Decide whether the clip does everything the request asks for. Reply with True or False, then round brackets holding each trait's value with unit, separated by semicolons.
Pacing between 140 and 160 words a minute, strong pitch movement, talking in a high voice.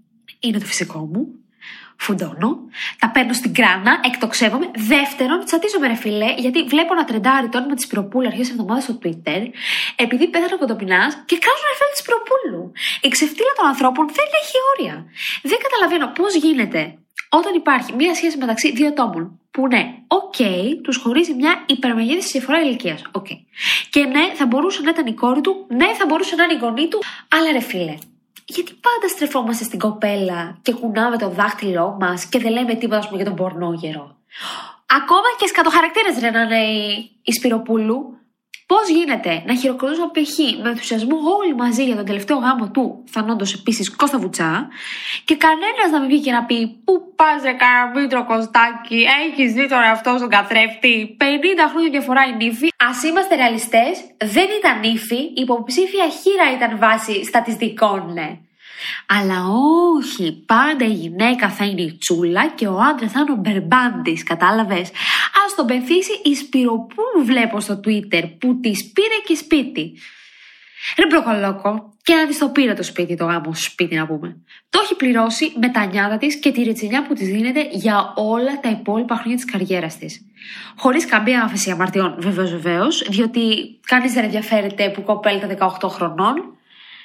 False (170 wpm; 6.1 semitones; 245 Hz)